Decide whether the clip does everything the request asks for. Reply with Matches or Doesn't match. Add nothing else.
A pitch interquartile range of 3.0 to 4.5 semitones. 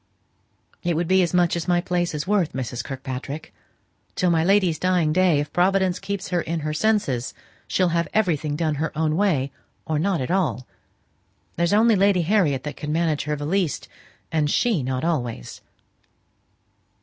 Matches